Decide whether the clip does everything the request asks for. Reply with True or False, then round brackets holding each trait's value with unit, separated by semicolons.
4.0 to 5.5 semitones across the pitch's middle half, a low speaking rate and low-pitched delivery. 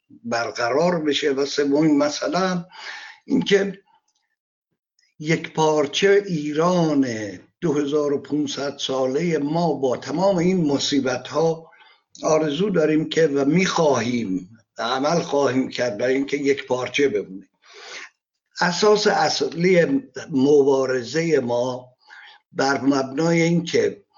False (4.3 semitones; 90 wpm; 150 Hz)